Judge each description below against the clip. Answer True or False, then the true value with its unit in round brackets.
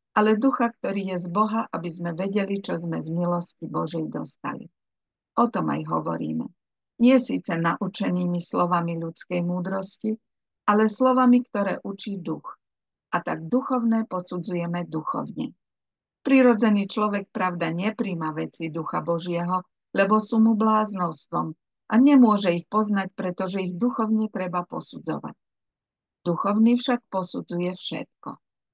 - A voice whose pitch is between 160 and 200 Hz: True (190 Hz)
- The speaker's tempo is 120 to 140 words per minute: True (125 wpm)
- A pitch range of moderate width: True (4.1 semitones)